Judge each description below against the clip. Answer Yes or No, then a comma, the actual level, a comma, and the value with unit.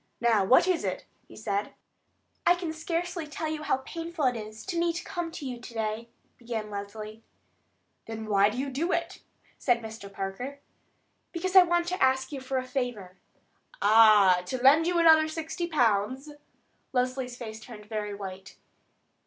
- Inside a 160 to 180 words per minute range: Yes, average, 170 wpm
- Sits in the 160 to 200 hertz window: No, very high, 255 Hz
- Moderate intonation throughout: No, wide, 6.7 semitones